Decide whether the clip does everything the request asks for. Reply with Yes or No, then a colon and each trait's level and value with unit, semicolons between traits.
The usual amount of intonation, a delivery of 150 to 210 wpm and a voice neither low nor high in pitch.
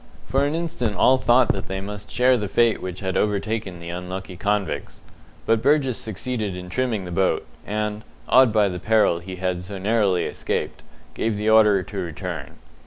No: average, 3.4 semitones; average, 180 wpm; low, 105 Hz